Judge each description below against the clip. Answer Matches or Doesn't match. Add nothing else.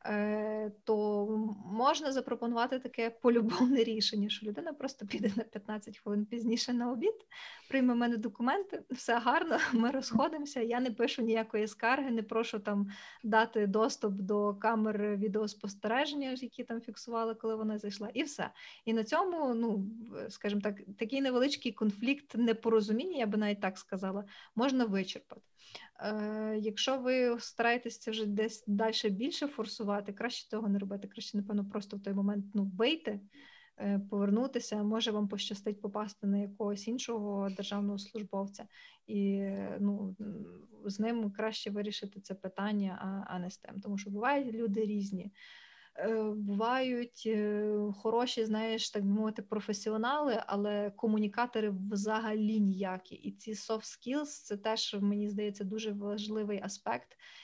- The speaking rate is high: Doesn't match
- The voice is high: Matches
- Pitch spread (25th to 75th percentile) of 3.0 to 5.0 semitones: Doesn't match